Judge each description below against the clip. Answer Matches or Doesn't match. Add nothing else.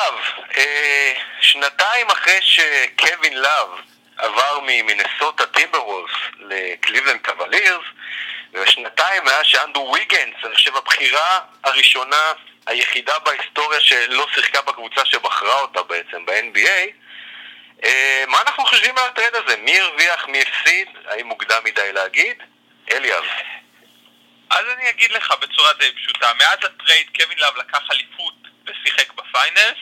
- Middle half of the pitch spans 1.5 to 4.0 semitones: Matches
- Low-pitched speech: Doesn't match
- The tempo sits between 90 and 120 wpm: Matches